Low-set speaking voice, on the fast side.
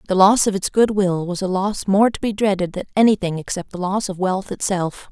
No: high, 195 Hz; fast, 245 wpm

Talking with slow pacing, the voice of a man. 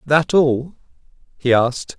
Yes: slow, 120 wpm; male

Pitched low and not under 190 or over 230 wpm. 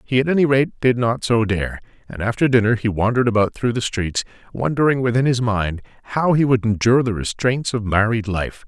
Yes: low, 115 Hz; average, 200 wpm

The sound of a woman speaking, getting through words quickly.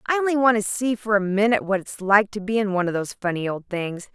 Yes: female; fast, 290 wpm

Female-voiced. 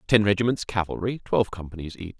No: male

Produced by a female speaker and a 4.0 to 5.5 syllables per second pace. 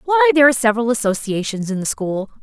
No: female; 6.9 syllables/s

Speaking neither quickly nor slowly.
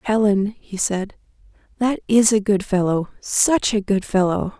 Yes: average, 155 wpm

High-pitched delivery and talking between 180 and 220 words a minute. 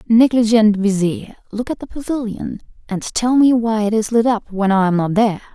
Yes: high, 220 Hz; fast, 205 wpm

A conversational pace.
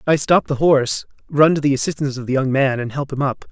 No: fast, 275 wpm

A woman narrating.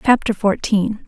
Yes: female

